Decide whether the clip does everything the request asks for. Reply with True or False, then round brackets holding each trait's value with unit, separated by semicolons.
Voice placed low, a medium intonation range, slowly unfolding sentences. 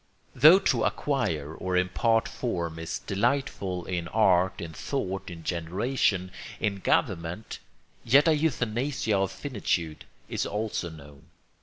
False (95 Hz; 6.0 semitones; 125 wpm)